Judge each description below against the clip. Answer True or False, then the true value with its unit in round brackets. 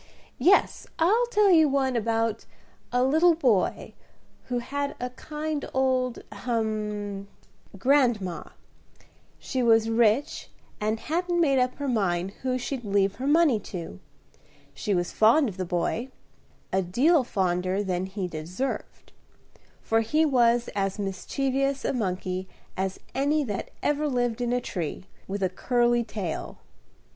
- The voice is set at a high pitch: True (240 Hz)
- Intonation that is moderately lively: False (5.7 semitones)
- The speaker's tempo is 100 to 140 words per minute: True (135 wpm)